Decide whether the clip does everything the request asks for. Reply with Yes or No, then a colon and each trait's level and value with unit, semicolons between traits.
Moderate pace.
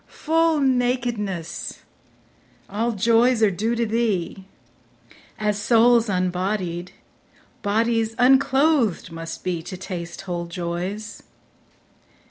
No: slow, 95 wpm